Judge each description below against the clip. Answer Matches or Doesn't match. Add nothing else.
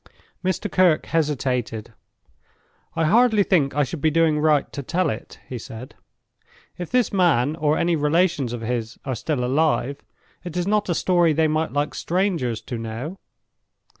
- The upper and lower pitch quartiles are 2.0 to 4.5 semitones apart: Doesn't match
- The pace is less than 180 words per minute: Matches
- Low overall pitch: Doesn't match